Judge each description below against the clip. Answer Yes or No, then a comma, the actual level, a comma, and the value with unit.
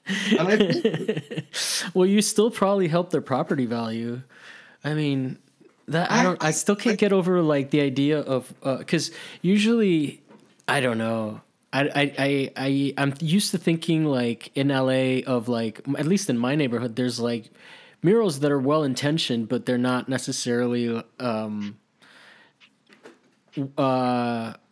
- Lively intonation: Yes, wide, 5.8 semitones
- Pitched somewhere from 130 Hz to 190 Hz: Yes, medium, 140 Hz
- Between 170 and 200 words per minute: No, average, 140 wpm